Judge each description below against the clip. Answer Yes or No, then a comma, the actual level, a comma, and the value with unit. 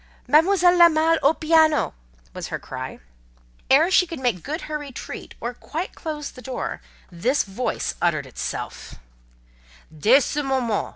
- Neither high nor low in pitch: No, very high, 295 Hz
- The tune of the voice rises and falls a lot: No, average, 4.3 semitones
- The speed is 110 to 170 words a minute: Yes, average, 150 wpm